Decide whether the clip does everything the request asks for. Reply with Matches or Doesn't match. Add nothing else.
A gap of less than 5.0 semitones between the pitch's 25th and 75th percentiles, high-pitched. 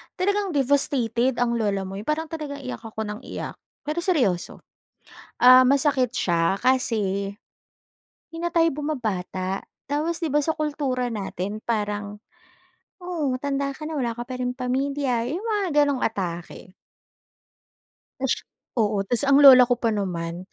Doesn't match